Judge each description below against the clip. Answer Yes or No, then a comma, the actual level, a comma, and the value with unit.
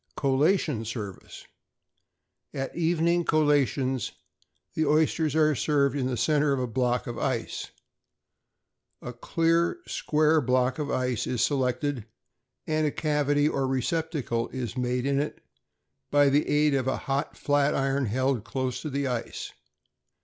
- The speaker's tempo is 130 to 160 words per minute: Yes, average, 140 wpm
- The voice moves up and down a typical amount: Yes, average, 3.0 semitones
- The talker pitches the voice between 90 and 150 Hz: Yes, medium, 140 Hz